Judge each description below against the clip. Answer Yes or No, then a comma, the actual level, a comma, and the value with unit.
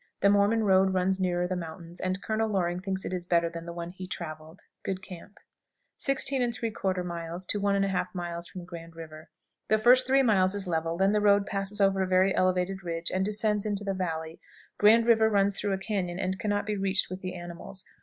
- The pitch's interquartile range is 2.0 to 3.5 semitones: Yes, average, 2.7 semitones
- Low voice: No, high, 190 Hz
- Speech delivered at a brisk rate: Yes, fast, 210 wpm